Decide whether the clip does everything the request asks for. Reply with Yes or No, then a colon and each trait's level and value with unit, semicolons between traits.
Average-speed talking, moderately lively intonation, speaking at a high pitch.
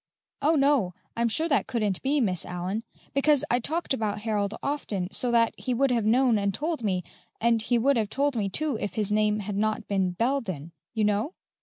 No: fast, 210 wpm; average, 5.0 semitones; high, 225 Hz